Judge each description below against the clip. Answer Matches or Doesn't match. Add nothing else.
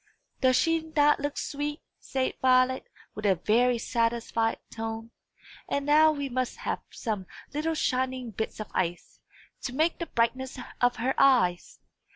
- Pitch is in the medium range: Doesn't match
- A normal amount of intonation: Matches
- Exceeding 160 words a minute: Doesn't match